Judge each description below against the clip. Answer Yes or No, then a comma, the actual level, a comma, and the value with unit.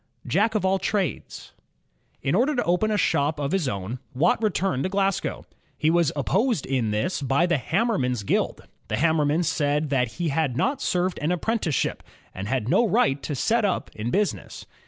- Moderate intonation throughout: No, wide, 6.3 semitones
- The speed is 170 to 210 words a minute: Yes, average, 180 wpm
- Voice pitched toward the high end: No, medium, 160 Hz